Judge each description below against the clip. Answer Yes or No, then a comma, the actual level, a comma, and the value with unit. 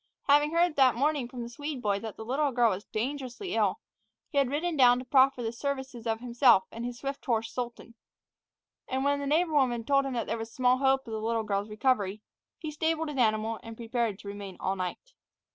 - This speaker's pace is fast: Yes, fast, 220 wpm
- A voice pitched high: Yes, high, 245 Hz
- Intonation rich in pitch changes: No, average, 3.8 semitones